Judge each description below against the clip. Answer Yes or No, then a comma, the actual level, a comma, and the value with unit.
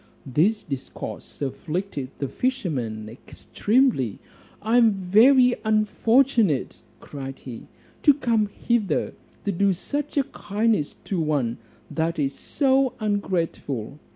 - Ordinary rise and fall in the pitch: No, wide, 8.5 semitones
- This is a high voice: Yes, high, 200 Hz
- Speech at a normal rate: No, slow, 110 wpm